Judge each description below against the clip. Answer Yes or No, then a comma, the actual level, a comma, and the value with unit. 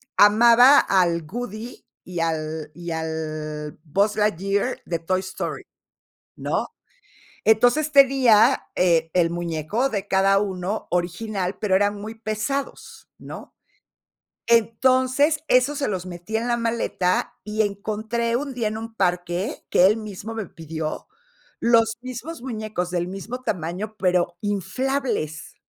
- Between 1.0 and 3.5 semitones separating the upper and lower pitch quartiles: No, average, 4.8 semitones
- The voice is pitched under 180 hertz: No, high, 205 Hz